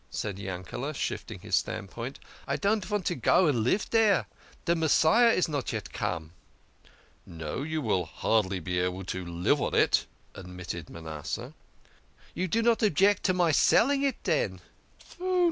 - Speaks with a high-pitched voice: No, low, 130 Hz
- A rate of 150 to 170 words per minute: Yes, average, 160 wpm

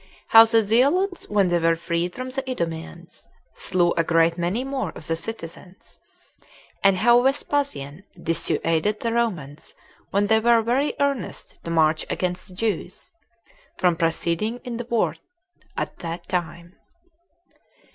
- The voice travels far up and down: Yes, wide, 6.0 semitones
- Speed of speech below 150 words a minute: Yes, average, 140 wpm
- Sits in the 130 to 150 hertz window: No, high, 190 Hz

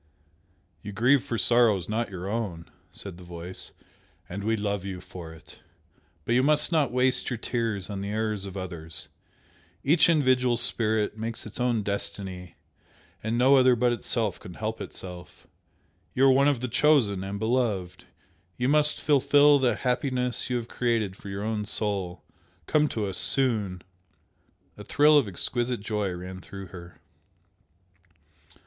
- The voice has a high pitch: No, low, 110 Hz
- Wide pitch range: No, average, 4.6 semitones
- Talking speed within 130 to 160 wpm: Yes, average, 155 wpm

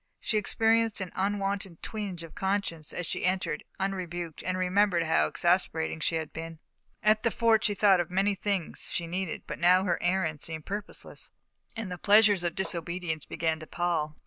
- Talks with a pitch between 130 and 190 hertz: Yes, medium, 185 Hz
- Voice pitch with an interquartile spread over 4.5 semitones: No, average, 3.4 semitones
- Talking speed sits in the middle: Yes, average, 180 wpm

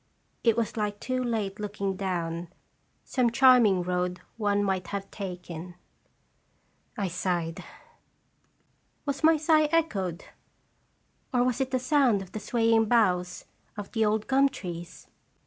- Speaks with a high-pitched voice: Yes, high, 210 Hz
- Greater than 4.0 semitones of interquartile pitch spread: Yes, wide, 5.4 semitones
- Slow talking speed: Yes, slow, 130 wpm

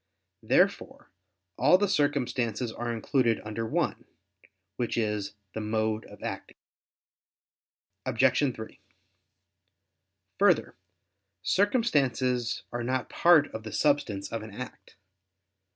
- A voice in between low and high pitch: No, low, 120 Hz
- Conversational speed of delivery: No, slow, 105 wpm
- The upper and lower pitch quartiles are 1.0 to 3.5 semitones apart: No, average, 4.3 semitones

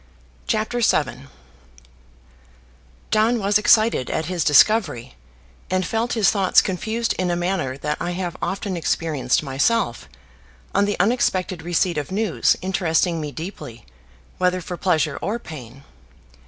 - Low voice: No, medium, 180 Hz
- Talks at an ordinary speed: No, slow, 130 wpm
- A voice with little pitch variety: No, average, 5.0 semitones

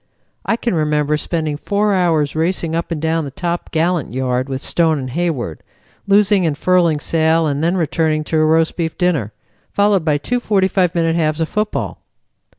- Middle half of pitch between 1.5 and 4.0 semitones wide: Yes, average, 2.8 semitones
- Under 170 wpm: No, average, 180 wpm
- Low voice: No, medium, 165 Hz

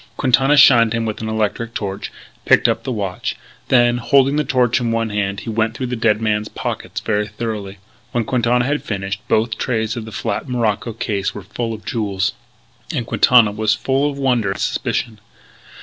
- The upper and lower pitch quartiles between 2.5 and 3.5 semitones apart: Yes, average, 2.8 semitones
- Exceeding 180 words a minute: Yes, average, 190 wpm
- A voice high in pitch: No, low, 115 Hz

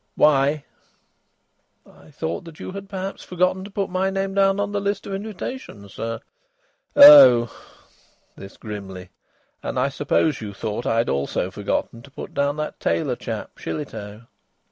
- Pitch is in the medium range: Yes, medium, 145 Hz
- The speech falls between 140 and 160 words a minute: Yes, average, 145 wpm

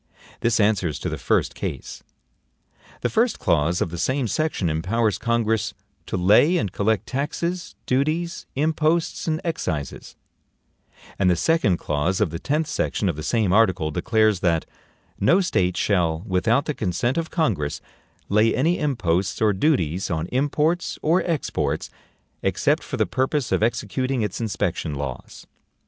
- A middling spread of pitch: No, wide, 8.6 semitones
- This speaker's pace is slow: No, average, 150 wpm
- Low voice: Yes, low, 110 Hz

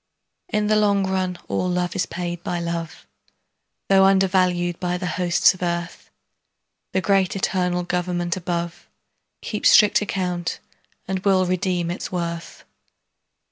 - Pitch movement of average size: No, narrow, 1.6 semitones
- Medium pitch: Yes, medium, 180 Hz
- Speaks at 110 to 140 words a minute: Yes, slow, 135 wpm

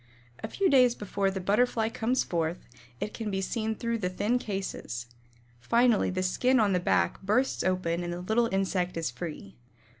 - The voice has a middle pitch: No, high, 195 Hz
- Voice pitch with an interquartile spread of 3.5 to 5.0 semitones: Yes, average, 4.2 semitones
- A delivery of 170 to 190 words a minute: Yes, average, 180 wpm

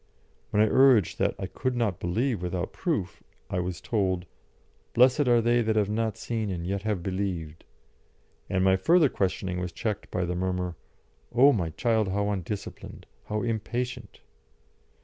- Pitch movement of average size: Yes, average, 4.3 semitones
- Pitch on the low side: Yes, low, 100 Hz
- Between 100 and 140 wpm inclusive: No, average, 160 wpm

